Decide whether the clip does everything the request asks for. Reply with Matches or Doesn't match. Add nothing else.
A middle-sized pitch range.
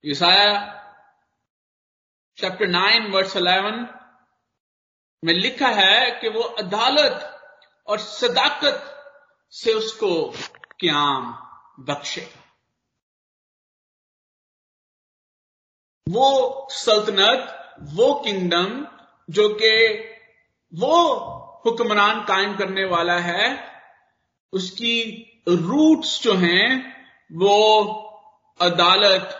Doesn't match